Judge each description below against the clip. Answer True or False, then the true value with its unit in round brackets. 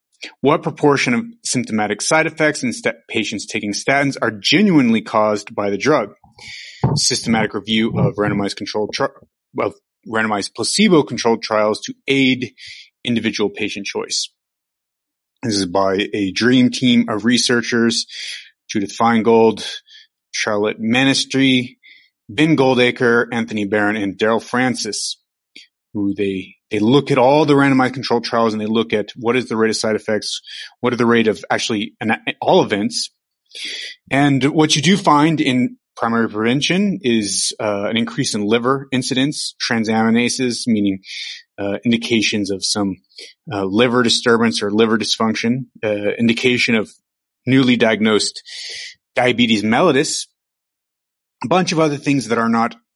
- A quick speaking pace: False (140 wpm)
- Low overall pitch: True (120 Hz)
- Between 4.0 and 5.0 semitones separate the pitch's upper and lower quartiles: True (4.3 semitones)